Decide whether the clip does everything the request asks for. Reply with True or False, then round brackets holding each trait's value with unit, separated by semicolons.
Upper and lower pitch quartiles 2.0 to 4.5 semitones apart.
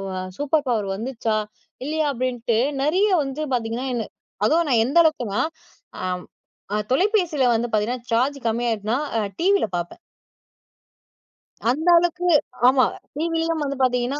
False (5.4 semitones)